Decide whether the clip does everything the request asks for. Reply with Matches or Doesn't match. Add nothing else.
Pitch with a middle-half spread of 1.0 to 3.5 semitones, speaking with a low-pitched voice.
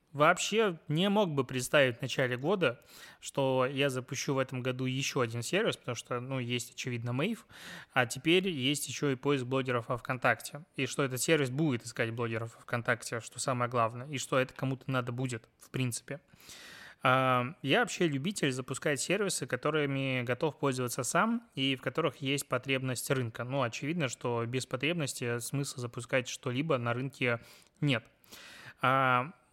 Matches